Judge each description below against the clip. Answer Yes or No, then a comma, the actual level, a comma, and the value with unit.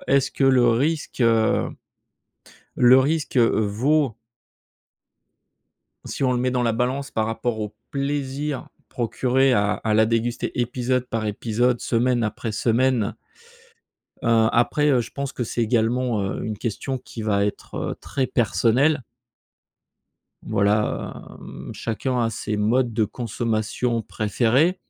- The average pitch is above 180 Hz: No, low, 120 Hz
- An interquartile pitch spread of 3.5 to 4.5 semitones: No, average, 2.8 semitones